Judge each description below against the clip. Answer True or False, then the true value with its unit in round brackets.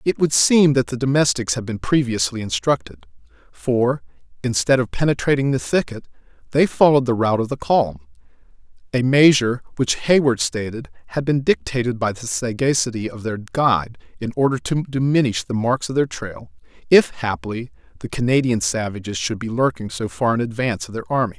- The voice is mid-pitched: False (120 Hz)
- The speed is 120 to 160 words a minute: False (170 wpm)